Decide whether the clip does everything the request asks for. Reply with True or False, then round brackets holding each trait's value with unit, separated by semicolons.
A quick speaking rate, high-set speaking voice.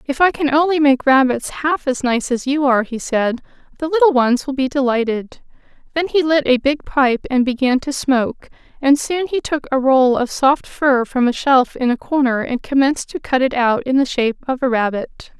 True (220 wpm; 265 Hz)